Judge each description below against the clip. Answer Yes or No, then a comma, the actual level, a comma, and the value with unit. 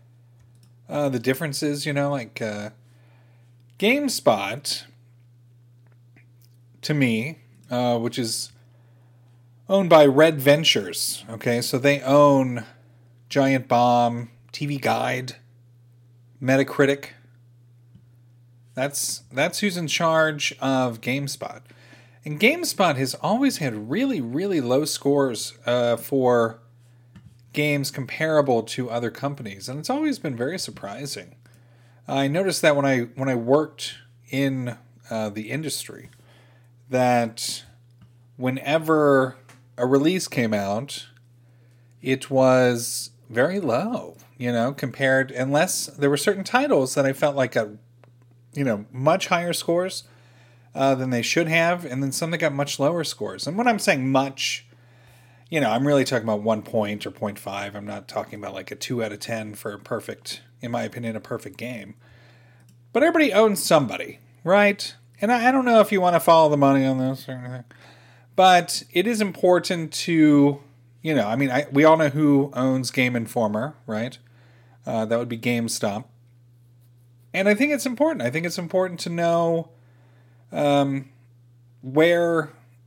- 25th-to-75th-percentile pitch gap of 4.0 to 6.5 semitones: No, average, 3.2 semitones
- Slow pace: No, average, 145 wpm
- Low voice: Yes, low, 125 Hz